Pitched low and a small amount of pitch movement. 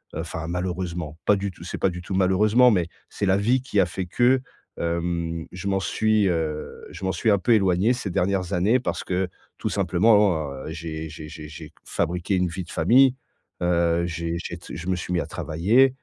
No: very low, 90 Hz; average, 3.1 semitones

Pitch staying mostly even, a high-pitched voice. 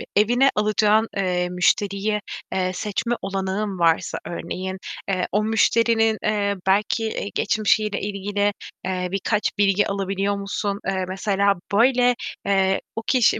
Yes: narrow, 1.9 semitones; high, 200 Hz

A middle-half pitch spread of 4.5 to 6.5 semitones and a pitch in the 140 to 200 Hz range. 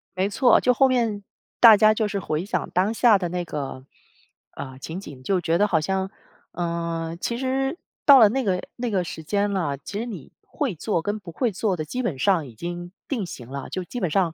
Yes: average, 4.9 semitones; high, 190 Hz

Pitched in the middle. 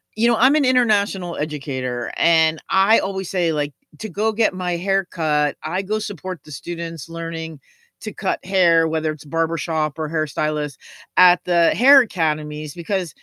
Yes: medium, 165 Hz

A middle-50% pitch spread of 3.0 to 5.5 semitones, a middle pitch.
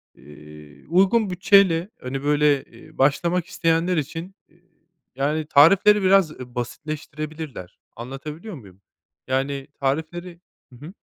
Yes: average, 4.5 semitones; medium, 155 Hz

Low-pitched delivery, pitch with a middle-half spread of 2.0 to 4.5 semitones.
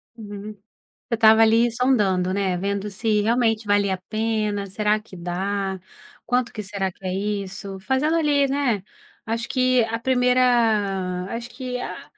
No: high, 215 Hz; average, 3.5 semitones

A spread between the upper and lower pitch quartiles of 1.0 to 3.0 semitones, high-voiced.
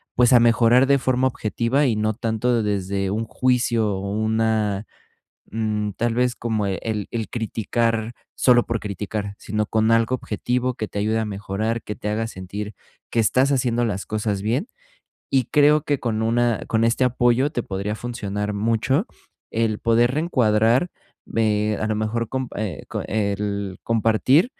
No: narrow, 2.4 semitones; low, 115 Hz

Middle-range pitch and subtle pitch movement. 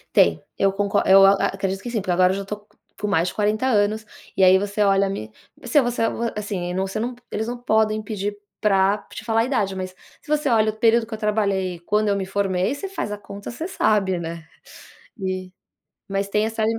No: high, 205 Hz; narrow, 2.3 semitones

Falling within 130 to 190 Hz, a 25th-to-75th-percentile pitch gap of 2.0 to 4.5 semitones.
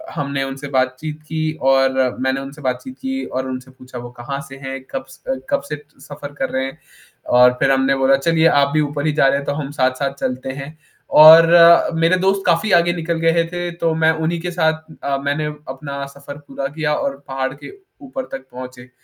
Yes: medium, 140 Hz; average, 3.2 semitones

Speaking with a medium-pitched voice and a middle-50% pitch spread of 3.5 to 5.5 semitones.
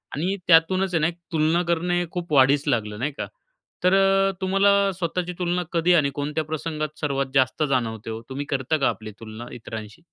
Yes: medium, 155 Hz; average, 4.9 semitones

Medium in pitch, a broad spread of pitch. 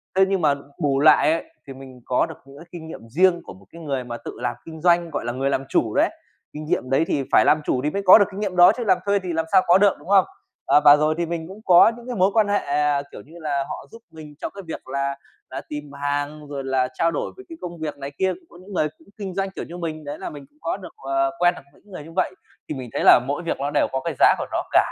No: medium, 155 Hz; average, 4.5 semitones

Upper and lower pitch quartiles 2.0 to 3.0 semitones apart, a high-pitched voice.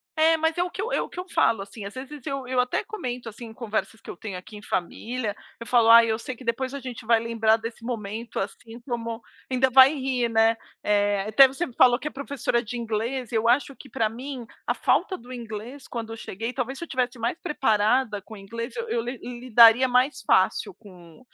Yes: average, 2.7 semitones; high, 235 Hz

